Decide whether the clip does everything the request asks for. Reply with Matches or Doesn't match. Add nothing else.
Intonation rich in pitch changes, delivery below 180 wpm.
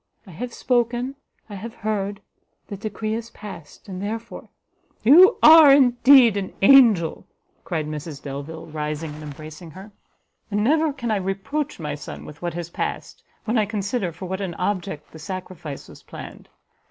Matches